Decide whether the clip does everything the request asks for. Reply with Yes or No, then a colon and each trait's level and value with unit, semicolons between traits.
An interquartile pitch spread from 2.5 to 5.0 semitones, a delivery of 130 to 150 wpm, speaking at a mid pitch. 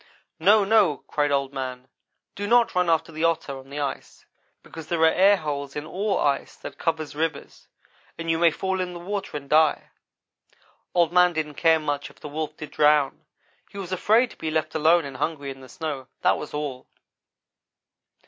No: average, 3.6 semitones; average, 195 wpm; medium, 160 Hz